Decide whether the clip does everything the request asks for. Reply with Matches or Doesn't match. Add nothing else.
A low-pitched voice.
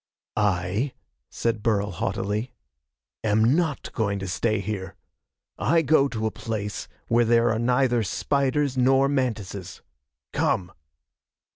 Matches